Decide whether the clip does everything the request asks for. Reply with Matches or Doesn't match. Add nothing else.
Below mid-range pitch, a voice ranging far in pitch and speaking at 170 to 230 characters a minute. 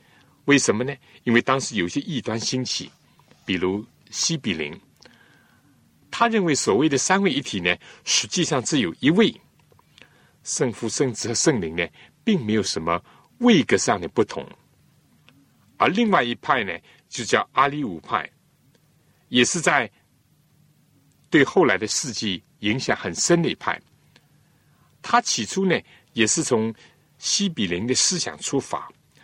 Matches